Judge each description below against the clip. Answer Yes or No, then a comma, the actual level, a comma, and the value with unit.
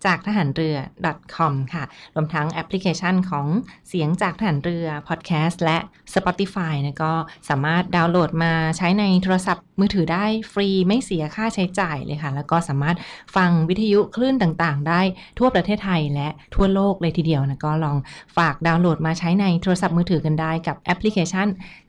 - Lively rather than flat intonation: No, average, 3.0 semitones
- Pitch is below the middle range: No, medium, 170 Hz